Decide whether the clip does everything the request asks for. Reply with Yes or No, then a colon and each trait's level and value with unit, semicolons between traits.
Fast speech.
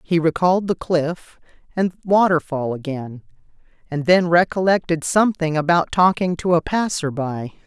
No: slow, 135 wpm